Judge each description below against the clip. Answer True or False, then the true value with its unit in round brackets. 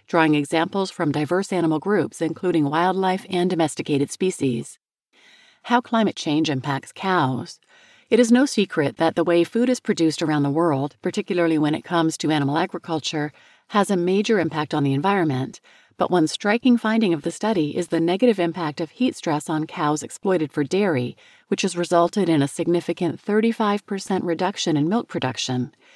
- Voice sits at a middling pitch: True (170 Hz)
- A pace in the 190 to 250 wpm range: False (170 wpm)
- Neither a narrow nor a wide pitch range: True (4.4 semitones)